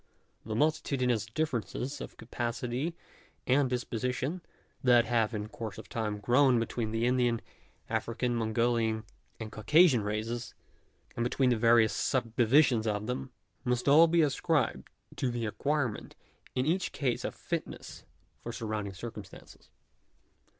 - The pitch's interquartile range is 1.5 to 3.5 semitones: Yes, average, 2.9 semitones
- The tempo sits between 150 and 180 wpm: No, slow, 135 wpm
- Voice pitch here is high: No, low, 120 Hz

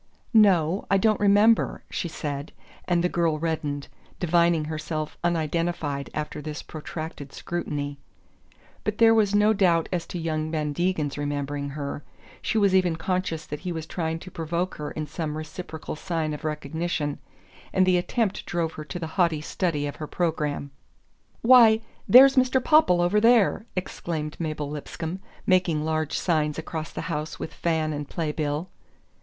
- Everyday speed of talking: Yes, average, 160 wpm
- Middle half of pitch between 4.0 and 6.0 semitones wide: No, average, 3.3 semitones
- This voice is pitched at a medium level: Yes, medium, 165 Hz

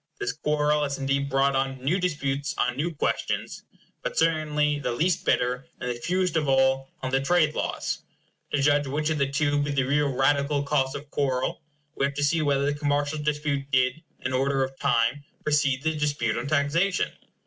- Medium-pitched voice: Yes, medium, 145 Hz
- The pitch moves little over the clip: Yes, narrow, 1.9 semitones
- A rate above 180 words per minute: Yes, average, 190 wpm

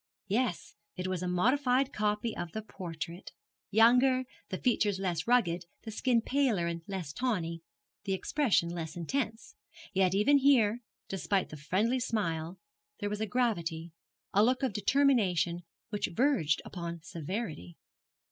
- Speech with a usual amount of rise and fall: No, wide, 6.0 semitones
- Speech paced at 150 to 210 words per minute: No, average, 140 wpm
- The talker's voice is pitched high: Yes, high, 205 Hz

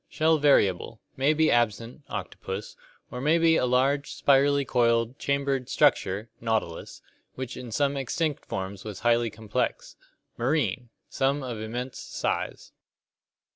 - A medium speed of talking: No, slow, 130 wpm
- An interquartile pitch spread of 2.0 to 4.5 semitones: Yes, average, 4.0 semitones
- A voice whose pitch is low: Yes, low, 125 Hz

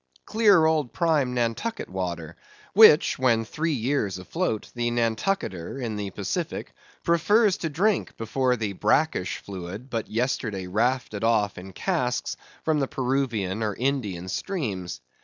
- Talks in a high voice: No, low, 120 Hz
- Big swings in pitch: Yes, wide, 7.1 semitones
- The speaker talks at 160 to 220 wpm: No, slow, 135 wpm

